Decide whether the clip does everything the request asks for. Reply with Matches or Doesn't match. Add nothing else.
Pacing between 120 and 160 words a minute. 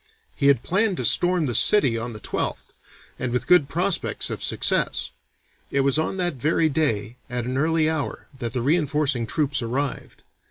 Doesn't match